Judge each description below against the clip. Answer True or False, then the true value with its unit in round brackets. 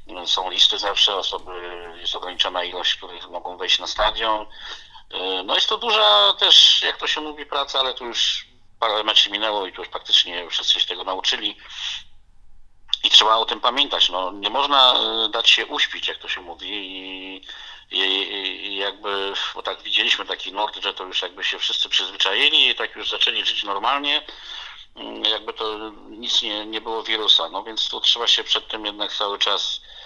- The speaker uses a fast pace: True (180 wpm)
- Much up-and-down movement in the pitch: True (7.9 semitones)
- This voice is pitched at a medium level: False (105 Hz)